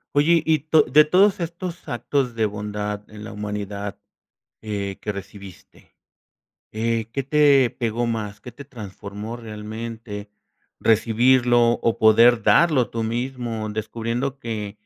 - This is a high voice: No, low, 115 Hz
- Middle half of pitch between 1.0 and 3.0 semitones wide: No, average, 3.6 semitones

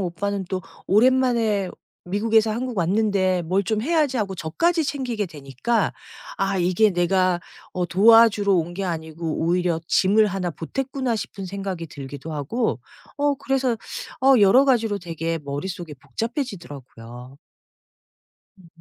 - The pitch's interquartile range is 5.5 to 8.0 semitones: No, average, 5.1 semitones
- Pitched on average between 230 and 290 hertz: No, high, 195 Hz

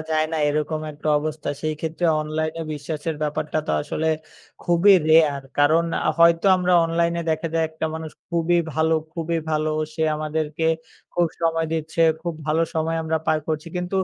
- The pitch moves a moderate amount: No, narrow, 1.2 semitones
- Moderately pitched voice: Yes, medium, 160 Hz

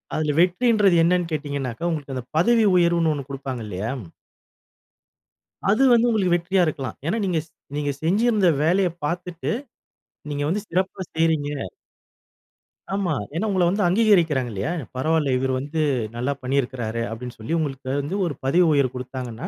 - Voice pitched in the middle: Yes, medium, 160 Hz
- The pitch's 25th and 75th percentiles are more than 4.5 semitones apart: Yes, average, 5.1 semitones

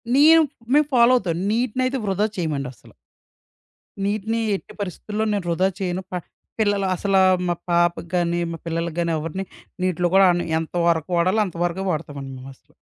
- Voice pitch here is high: No, medium, 180 Hz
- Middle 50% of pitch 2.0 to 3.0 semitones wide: No, average, 3.5 semitones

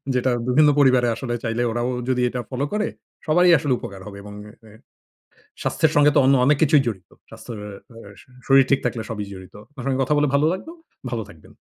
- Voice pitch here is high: No, low, 130 Hz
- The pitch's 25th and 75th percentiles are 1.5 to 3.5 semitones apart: No, average, 4.0 semitones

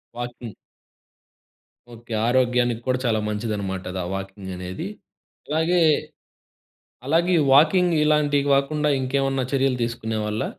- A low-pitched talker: Yes, low, 125 Hz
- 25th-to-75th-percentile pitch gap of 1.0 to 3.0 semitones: No, average, 5.0 semitones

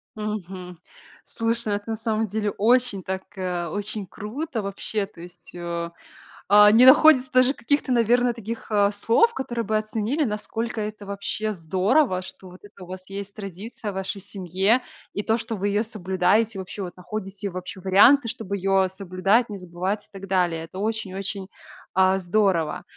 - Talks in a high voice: Yes, high, 205 Hz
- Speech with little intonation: No, average, 3.0 semitones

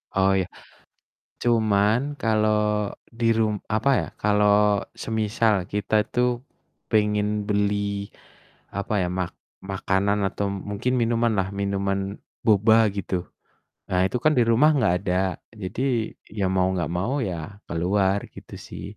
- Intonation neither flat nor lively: No, narrow, 2.1 semitones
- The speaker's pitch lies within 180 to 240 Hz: No, low, 105 Hz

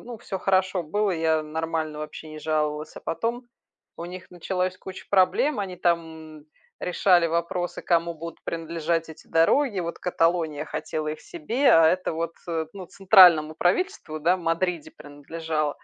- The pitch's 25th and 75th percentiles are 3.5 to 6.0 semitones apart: No, average, 2.7 semitones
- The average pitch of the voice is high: No, medium, 170 Hz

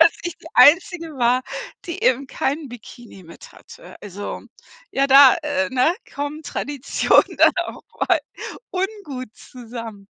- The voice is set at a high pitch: Yes, very high, 275 Hz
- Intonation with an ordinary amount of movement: Yes, average, 4.7 semitones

